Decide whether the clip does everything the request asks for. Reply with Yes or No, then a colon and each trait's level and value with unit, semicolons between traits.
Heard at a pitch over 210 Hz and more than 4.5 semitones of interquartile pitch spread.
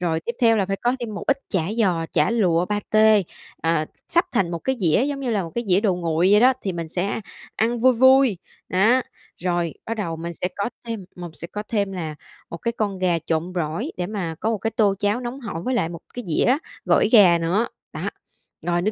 No: high, 195 Hz; average, 5.0 semitones